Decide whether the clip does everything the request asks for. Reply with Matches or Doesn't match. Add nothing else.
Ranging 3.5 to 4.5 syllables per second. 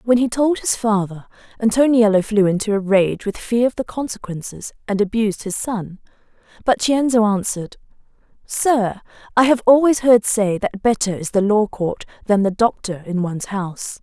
Doesn't match